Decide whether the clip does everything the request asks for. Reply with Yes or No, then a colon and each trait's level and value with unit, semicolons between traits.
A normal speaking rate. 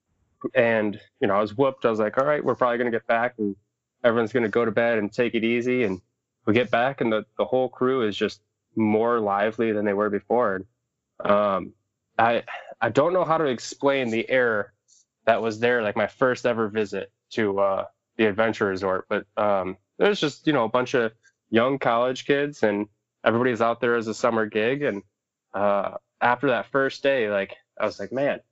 No: fast, 210 wpm